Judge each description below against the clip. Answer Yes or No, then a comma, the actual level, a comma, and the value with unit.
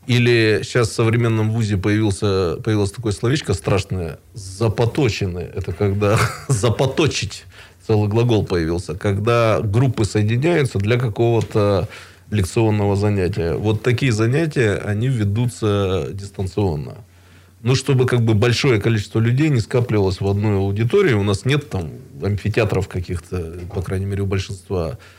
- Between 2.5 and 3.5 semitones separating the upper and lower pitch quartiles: Yes, average, 3.2 semitones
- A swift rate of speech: No, average, 125 wpm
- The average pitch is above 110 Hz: No, low, 105 Hz